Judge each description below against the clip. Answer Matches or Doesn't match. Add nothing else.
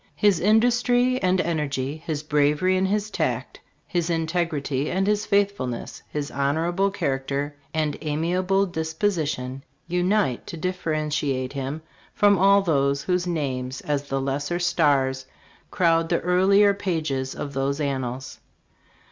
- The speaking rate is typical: Doesn't match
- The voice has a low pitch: Doesn't match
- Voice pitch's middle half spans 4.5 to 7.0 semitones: Matches